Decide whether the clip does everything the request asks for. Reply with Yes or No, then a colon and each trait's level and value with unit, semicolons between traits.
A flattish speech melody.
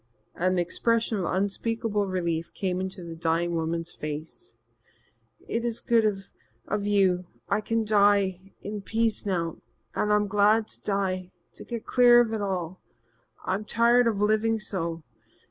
No: average, 3.5 semitones